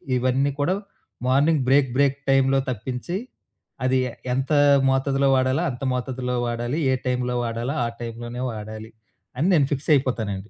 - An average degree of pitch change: No, narrow, 2.3 semitones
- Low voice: Yes, low, 130 Hz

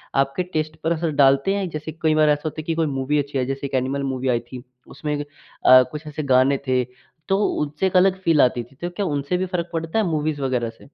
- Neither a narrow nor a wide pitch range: Yes, average, 3.3 semitones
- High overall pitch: No, medium, 150 Hz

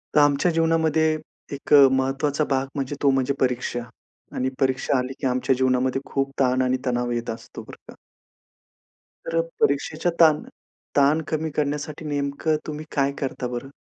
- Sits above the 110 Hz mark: Yes, medium, 140 Hz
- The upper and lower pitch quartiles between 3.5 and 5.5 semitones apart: No, average, 2.7 semitones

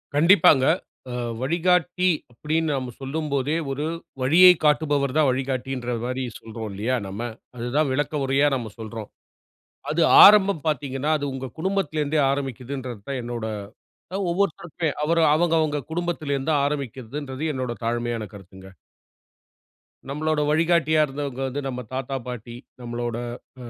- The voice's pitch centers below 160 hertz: Yes, medium, 140 Hz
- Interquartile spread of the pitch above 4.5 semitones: No, average, 3.9 semitones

